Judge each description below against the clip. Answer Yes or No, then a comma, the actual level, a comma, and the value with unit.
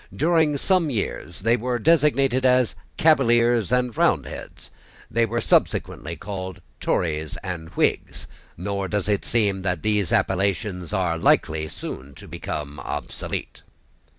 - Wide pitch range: Yes, wide, 5.8 semitones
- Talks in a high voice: No, low, 105 Hz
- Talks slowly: Yes, slow, 125 wpm